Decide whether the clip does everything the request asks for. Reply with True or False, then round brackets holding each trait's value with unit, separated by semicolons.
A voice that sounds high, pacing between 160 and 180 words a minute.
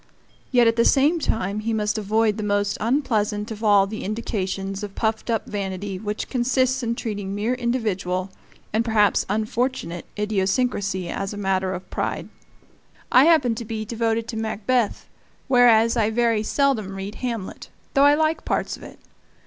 True (220 Hz; 165 wpm)